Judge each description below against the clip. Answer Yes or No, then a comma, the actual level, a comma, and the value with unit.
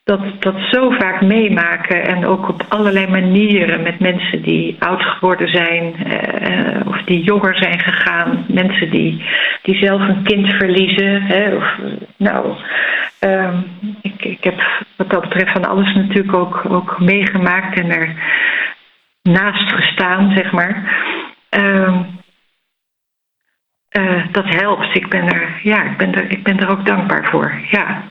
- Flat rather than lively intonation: Yes, narrow, 1.8 semitones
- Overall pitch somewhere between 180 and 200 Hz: Yes, high, 190 Hz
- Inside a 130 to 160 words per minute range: Yes, average, 145 wpm